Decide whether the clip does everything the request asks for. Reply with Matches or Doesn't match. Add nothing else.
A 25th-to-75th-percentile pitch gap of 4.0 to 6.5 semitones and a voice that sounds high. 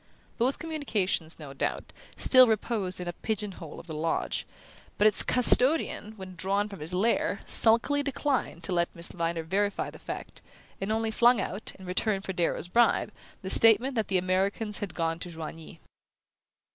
Matches